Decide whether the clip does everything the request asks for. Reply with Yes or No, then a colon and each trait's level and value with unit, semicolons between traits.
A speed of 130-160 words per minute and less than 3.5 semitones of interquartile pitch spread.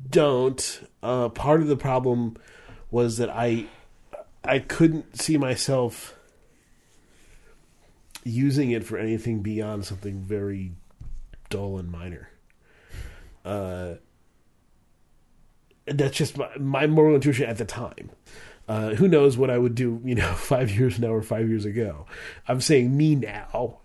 No: slow, 135 wpm; average, 4.0 semitones